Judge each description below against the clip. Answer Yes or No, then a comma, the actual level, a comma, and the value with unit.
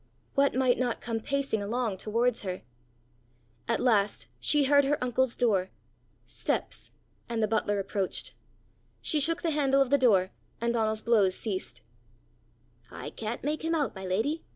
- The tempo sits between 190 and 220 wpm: No, average, 155 wpm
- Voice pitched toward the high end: Yes, high, 235 Hz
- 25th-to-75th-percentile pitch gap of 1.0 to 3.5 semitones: No, average, 4.9 semitones